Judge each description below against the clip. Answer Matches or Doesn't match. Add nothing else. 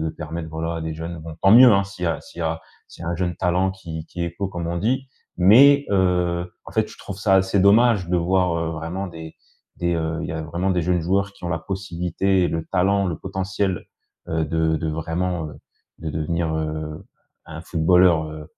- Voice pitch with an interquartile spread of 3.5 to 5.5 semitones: Doesn't match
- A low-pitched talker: Matches